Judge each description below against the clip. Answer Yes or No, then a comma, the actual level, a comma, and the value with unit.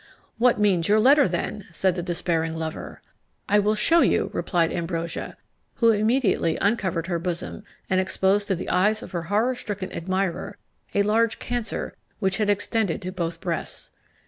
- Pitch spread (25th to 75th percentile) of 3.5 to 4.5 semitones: Yes, average, 3.8 semitones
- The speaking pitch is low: No, high, 190 Hz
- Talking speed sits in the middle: Yes, average, 165 wpm